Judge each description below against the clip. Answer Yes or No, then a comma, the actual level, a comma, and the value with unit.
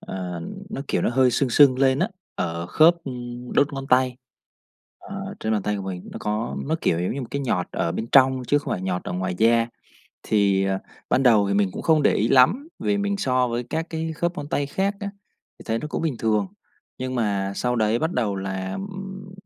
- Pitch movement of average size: No, wide, 6.4 semitones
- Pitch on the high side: No, low, 125 Hz